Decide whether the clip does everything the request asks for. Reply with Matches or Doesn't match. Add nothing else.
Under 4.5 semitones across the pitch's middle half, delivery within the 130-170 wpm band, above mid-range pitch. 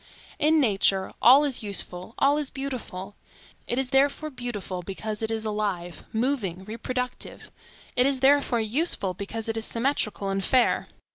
Doesn't match